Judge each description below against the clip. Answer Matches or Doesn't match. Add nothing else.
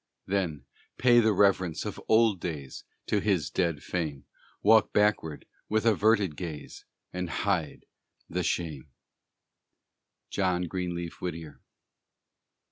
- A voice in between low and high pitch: Doesn't match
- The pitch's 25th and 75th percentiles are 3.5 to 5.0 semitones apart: Matches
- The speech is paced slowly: Matches